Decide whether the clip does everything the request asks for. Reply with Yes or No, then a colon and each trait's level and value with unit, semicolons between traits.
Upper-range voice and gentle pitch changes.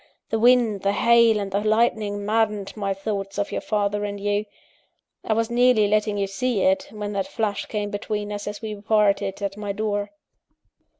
Yes: high, 210 Hz; narrow, 1.4 semitones